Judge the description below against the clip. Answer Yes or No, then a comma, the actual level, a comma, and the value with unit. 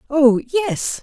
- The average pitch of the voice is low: No, very high, 290 Hz